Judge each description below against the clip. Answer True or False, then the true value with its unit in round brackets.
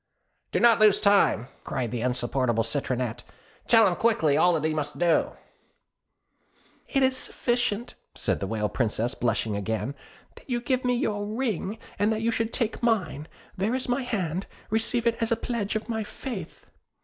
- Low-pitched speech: False (205 Hz)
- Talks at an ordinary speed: True (175 wpm)